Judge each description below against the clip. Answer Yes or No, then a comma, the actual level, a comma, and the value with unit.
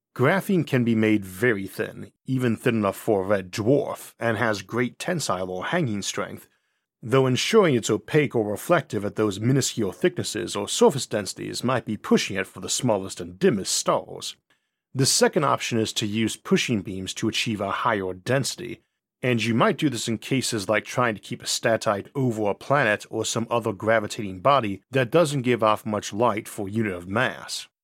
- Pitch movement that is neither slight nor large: Yes, average, 3.7 semitones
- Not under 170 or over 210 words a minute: Yes, average, 190 wpm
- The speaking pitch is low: Yes, low, 115 Hz